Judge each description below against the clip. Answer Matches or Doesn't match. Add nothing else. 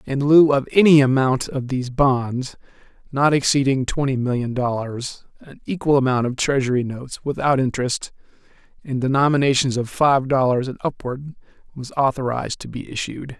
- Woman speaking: Doesn't match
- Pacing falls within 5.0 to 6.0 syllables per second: Matches